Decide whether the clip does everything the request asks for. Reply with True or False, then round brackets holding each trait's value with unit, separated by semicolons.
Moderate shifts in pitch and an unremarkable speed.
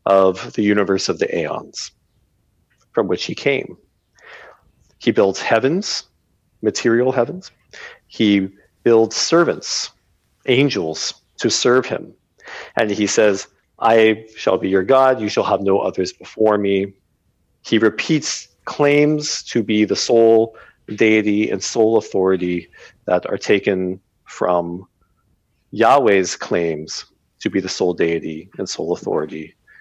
False (3.6 semitones; 125 wpm)